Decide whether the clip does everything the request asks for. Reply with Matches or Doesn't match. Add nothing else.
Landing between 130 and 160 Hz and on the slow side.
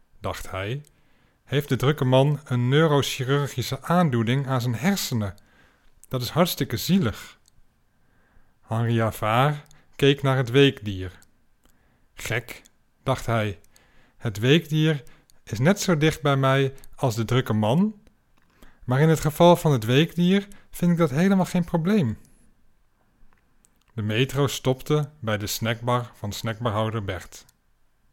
Matches